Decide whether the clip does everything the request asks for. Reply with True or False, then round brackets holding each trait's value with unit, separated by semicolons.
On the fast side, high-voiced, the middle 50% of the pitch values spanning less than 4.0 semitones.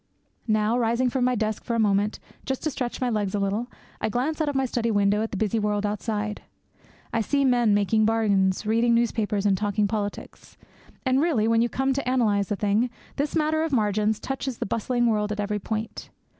True (210 wpm; 220 Hz; 3.0 semitones)